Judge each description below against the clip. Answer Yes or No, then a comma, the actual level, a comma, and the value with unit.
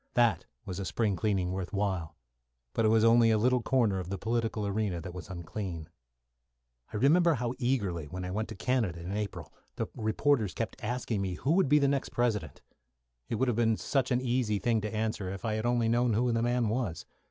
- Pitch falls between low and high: No, low, 110 Hz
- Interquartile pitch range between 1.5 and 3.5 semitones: No, average, 4.0 semitones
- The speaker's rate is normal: No, fast, 215 wpm